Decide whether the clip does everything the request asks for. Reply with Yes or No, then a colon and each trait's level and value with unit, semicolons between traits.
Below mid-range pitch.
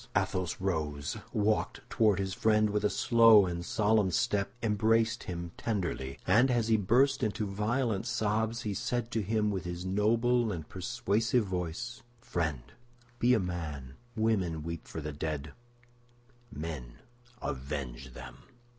Yes: low, 100 Hz